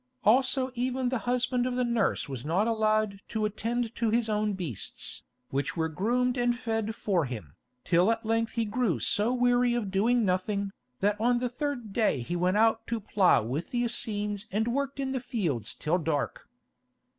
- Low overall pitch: No, high, 220 Hz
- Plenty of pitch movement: No, average, 4.3 semitones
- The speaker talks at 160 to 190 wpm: Yes, average, 185 wpm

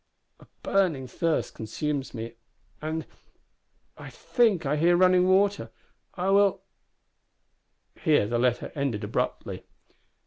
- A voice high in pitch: No, medium, 155 Hz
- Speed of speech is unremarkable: No, slow, 115 wpm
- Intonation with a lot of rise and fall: Yes, wide, 6.4 semitones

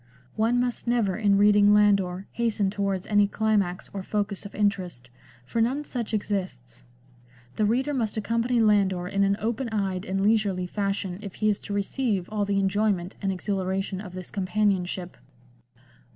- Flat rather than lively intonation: Yes, narrow, 2.3 semitones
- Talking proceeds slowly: No, average, 160 wpm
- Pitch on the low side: No, high, 200 Hz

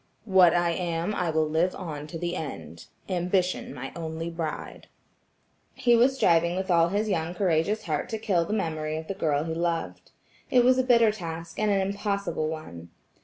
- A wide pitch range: No, average, 3.7 semitones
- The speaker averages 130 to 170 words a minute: No, average, 180 wpm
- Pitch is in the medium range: Yes, medium, 170 Hz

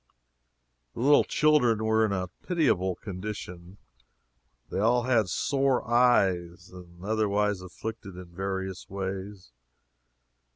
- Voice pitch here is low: Yes, low, 100 Hz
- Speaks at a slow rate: Yes, slow, 115 wpm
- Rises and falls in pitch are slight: No, average, 3.7 semitones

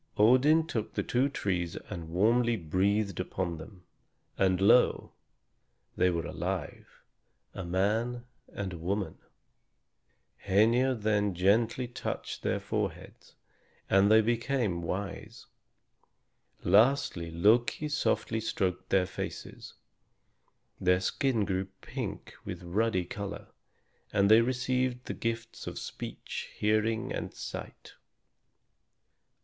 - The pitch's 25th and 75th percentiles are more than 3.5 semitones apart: Yes, average, 4.3 semitones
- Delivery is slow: Yes, slow, 110 wpm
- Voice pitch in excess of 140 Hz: No, low, 105 Hz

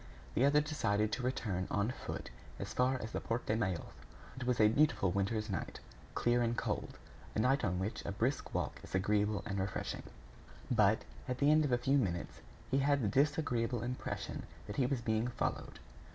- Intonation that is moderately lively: Yes, average, 4.1 semitones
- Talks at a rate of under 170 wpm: No, average, 190 wpm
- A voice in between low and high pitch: No, low, 115 Hz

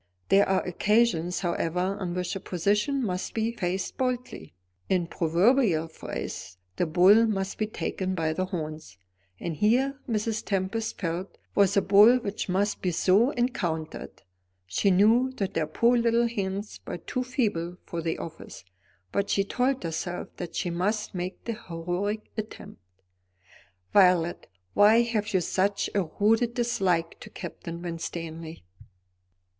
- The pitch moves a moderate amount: Yes, average, 4.3 semitones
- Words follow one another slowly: No, average, 145 wpm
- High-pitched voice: Yes, high, 195 Hz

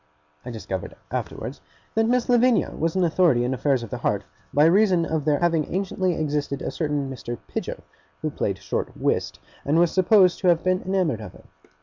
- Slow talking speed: No, average, 195 wpm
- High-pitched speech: No, medium, 160 Hz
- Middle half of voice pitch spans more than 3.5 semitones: Yes, average, 5.2 semitones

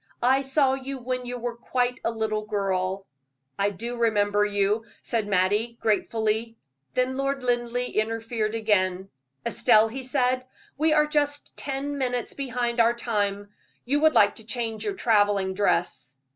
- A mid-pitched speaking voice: No, high, 230 Hz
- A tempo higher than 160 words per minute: No, average, 150 wpm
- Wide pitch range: No, average, 3.6 semitones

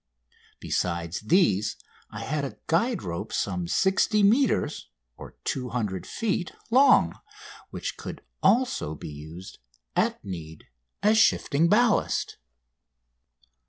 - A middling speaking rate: No, slow, 100 wpm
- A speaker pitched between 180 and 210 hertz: No, low, 135 Hz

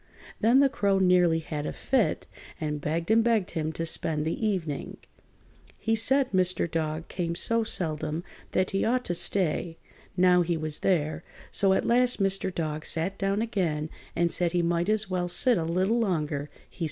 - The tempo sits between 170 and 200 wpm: Yes, average, 185 wpm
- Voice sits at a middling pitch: Yes, medium, 180 Hz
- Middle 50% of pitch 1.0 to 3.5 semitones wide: No, average, 4.0 semitones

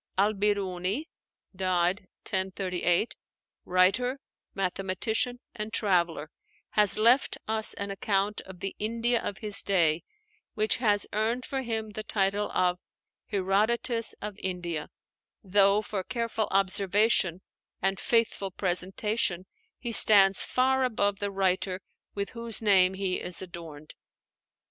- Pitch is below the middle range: No, high, 200 Hz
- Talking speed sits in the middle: No, slow, 115 wpm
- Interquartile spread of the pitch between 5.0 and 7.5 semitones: No, average, 2.8 semitones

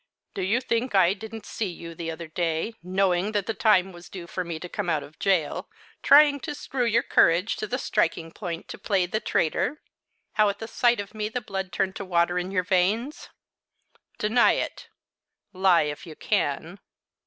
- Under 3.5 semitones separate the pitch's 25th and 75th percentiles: No, average, 4.1 semitones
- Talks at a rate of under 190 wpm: No, average, 195 wpm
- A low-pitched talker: No, high, 190 Hz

